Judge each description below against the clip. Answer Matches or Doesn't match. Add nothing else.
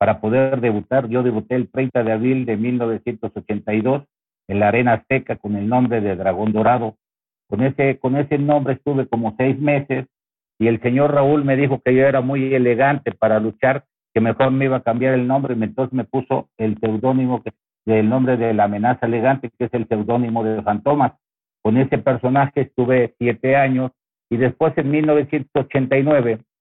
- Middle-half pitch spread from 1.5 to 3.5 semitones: Matches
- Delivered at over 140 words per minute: Matches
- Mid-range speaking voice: Doesn't match